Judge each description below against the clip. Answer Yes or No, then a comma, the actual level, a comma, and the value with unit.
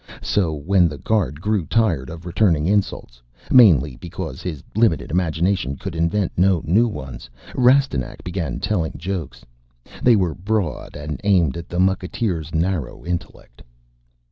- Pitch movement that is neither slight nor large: Yes, average, 4.3 semitones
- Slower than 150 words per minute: Yes, average, 140 wpm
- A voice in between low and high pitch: No, very low, 85 Hz